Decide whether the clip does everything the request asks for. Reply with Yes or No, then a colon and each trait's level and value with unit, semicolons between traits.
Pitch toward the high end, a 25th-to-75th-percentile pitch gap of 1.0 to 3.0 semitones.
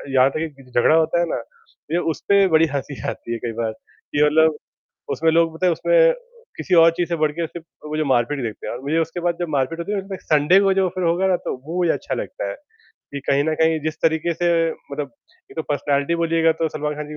No: medium, 160 Hz; narrow, 2.6 semitones